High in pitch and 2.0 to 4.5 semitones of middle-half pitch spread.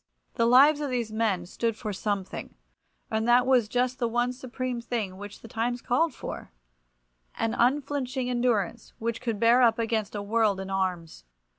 Yes: high, 230 Hz; average, 3.5 semitones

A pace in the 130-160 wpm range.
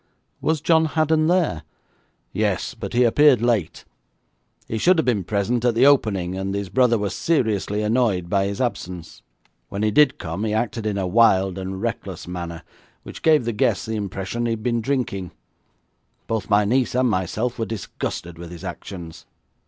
No: average, 180 wpm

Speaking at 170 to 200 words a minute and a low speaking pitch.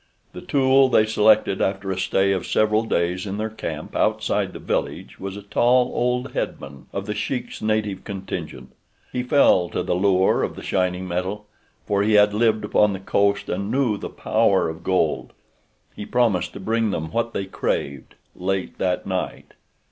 Yes: average, 180 wpm; low, 100 Hz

